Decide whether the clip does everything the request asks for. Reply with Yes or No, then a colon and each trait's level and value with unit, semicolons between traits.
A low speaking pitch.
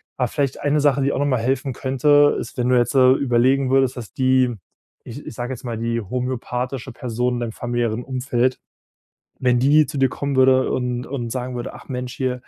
Yes: low, 130 Hz